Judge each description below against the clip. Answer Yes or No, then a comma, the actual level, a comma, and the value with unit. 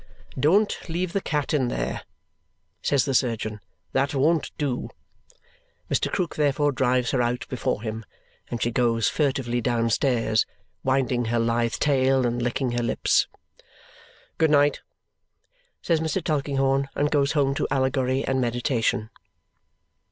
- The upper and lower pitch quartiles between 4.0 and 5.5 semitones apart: No, average, 3.3 semitones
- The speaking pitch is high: No, low, 130 Hz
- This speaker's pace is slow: Yes, slow, 130 wpm